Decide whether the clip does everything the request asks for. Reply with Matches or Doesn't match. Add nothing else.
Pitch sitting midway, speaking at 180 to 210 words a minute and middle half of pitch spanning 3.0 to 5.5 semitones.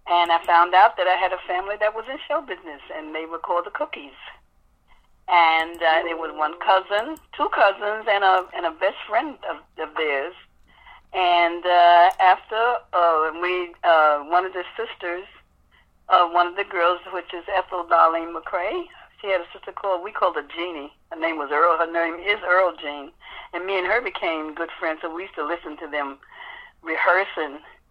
Doesn't match